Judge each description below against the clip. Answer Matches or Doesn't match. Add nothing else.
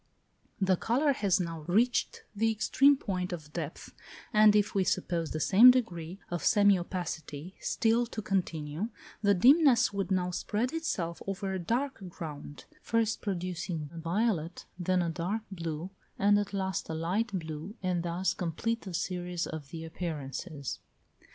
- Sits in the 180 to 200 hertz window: Matches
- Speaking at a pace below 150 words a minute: Doesn't match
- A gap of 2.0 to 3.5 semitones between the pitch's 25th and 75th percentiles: Doesn't match